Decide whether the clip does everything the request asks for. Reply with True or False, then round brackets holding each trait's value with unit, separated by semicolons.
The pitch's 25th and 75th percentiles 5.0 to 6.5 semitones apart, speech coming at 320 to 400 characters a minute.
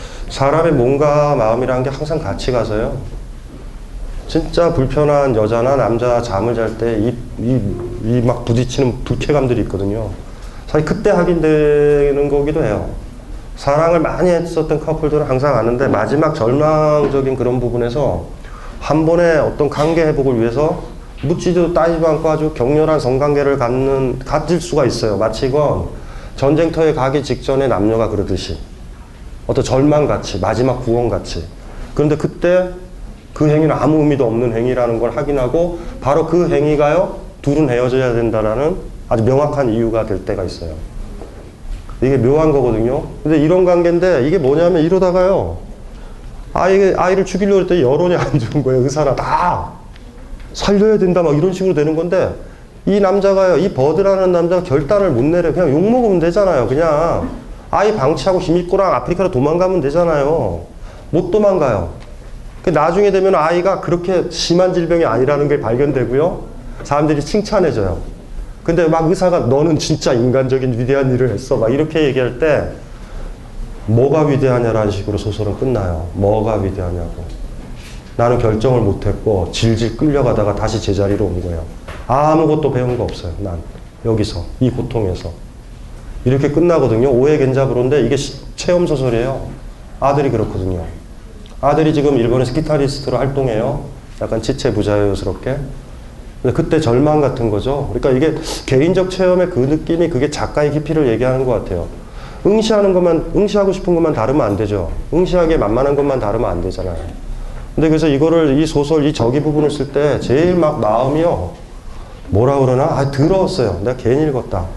True (5.6 semitones; 345 characters per minute)